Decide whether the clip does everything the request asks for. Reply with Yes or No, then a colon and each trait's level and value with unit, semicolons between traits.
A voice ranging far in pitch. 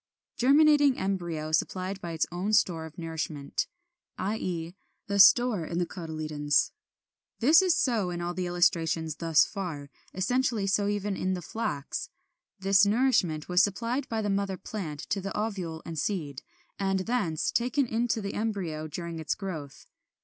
No: average, 4.7 semitones